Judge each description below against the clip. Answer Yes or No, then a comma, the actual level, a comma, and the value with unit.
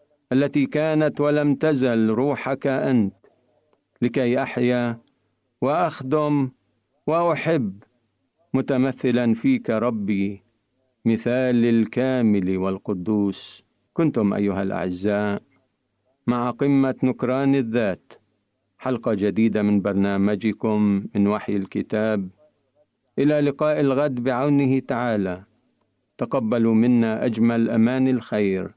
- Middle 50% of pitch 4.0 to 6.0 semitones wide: Yes, average, 4.4 semitones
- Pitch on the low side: Yes, low, 120 Hz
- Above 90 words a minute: No, average, 85 wpm